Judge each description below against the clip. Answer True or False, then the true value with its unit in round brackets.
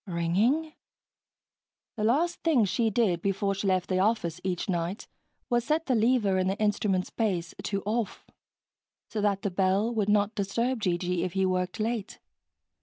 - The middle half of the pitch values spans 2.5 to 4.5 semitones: True (3.6 semitones)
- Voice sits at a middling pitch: False (200 Hz)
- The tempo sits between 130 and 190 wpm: True (165 wpm)